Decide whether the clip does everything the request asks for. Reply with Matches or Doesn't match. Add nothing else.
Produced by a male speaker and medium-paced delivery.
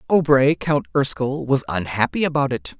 Matches